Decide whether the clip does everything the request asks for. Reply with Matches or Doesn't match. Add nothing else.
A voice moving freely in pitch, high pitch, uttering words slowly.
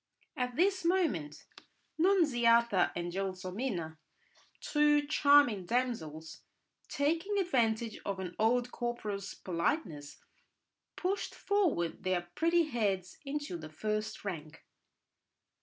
Matches